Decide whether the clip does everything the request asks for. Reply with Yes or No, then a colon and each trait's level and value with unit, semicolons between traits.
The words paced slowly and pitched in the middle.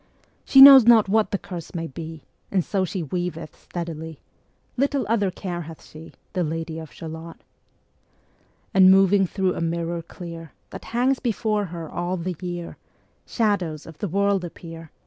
No: average, 170 wpm; medium, 175 Hz